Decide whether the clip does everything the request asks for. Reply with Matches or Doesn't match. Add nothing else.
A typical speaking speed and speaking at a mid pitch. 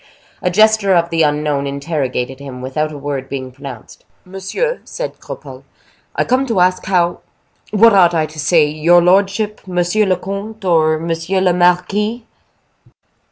Matches